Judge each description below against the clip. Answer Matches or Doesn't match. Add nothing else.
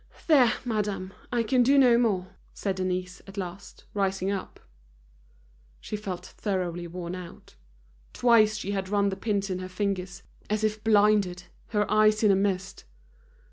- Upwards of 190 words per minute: Doesn't match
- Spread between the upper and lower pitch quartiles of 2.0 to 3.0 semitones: Matches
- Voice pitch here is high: Matches